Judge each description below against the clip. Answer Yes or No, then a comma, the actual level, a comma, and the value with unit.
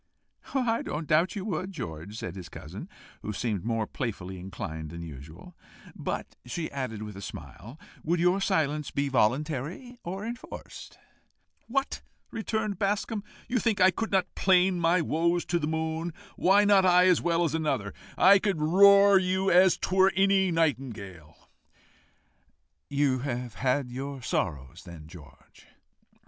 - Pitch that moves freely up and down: Yes, wide, 8.8 semitones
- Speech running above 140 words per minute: Yes, average, 150 wpm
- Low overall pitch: No, medium, 160 Hz